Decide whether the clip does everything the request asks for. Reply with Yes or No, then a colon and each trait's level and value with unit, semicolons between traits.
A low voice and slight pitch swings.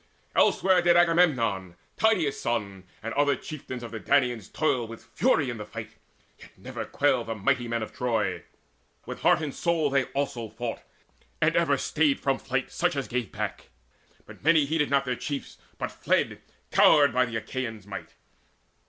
No: low, 130 Hz; average, 4.2 semitones